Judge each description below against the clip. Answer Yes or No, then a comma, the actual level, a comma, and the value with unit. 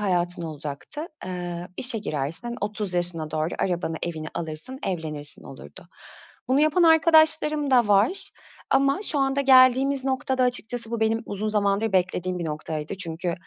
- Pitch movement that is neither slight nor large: No, wide, 7.4 semitones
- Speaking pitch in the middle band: No, high, 205 Hz